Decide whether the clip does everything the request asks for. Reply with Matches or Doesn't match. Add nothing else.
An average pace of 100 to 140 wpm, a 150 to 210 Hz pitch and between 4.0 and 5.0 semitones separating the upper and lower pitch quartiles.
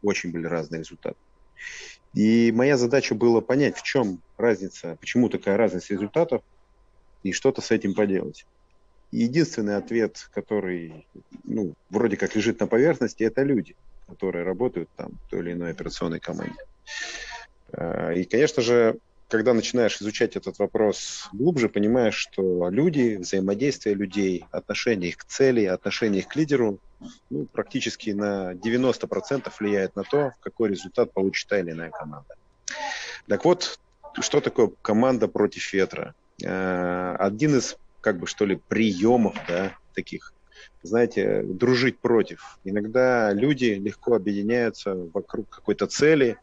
Doesn't match